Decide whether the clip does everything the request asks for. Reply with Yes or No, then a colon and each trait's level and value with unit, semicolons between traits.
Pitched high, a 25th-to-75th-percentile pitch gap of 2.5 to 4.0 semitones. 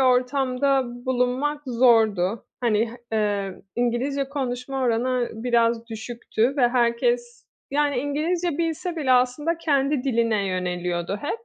Yes: very high, 250 Hz; average, 3.3 semitones